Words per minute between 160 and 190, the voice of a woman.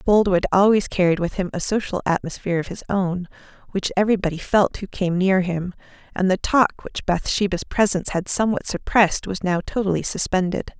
Yes: average, 170 wpm; female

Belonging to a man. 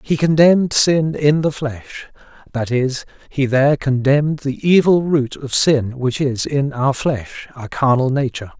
Yes: male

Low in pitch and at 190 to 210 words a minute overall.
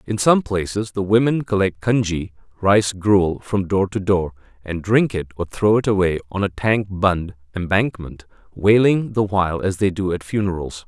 No: very low, 95 Hz; average, 180 wpm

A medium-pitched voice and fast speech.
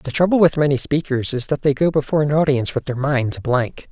Yes: medium, 145 Hz; fast, 260 wpm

